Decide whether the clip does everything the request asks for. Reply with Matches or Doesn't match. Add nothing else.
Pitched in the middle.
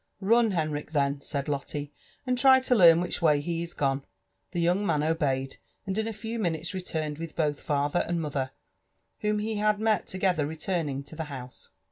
Matches